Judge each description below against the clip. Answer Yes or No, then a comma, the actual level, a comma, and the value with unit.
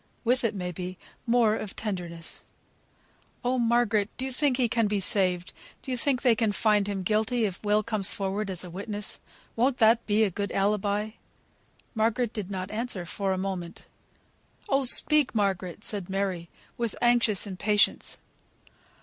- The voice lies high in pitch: Yes, high, 210 Hz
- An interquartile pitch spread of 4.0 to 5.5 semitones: No, average, 3.3 semitones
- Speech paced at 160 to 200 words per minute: Yes, average, 165 wpm